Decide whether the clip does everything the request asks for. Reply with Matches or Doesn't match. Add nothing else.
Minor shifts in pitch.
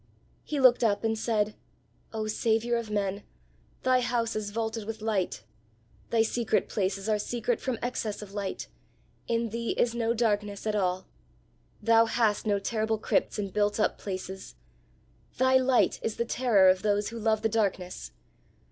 Matches